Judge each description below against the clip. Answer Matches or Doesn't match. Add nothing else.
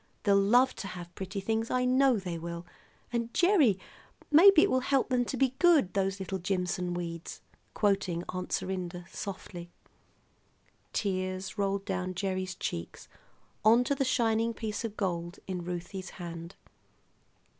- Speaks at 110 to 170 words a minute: Matches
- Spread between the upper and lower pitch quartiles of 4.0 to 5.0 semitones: Matches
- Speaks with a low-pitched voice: Doesn't match